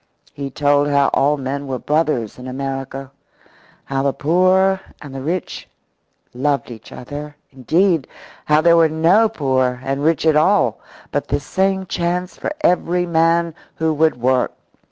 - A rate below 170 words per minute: Yes, average, 155 wpm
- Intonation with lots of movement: No, average, 4.0 semitones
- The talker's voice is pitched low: No, medium, 150 Hz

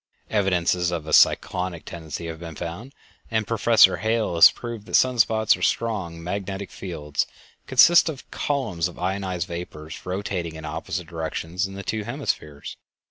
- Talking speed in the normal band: Yes, average, 160 wpm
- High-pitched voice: No, very low, 90 Hz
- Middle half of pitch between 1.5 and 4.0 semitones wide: No, average, 4.6 semitones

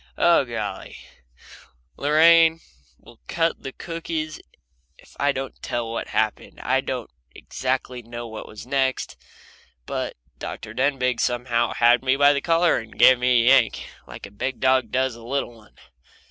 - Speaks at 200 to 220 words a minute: No, average, 160 wpm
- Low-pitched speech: Yes, low, 130 Hz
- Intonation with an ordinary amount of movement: Yes, average, 3.2 semitones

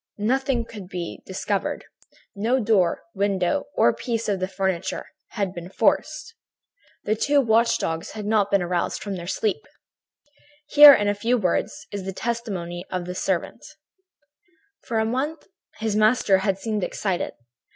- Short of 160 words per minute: Yes, average, 150 wpm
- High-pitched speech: Yes, high, 205 Hz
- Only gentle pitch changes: No, average, 3.6 semitones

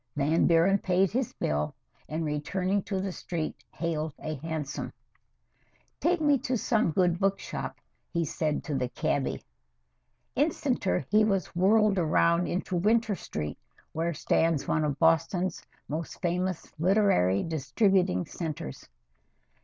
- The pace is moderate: No, slow, 130 wpm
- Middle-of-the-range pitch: Yes, medium, 170 Hz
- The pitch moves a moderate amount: Yes, average, 4.1 semitones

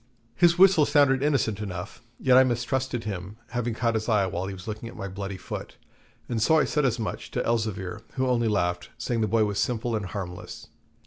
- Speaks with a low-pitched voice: Yes, low, 115 Hz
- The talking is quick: Yes, fast, 210 wpm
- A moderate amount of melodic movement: Yes, average, 4.4 semitones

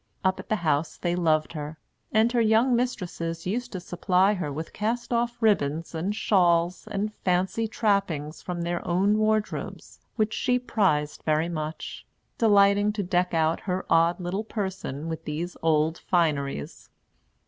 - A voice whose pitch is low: No, medium, 180 Hz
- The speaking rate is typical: Yes, average, 155 wpm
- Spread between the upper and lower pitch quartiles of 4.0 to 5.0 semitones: Yes, average, 4.5 semitones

